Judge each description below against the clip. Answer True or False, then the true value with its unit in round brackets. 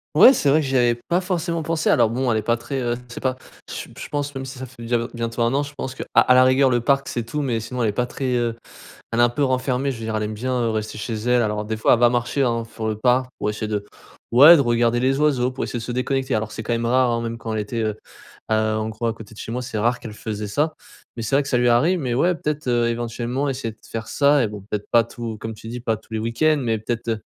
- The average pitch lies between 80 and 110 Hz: False (120 Hz)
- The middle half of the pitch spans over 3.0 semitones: False (2.7 semitones)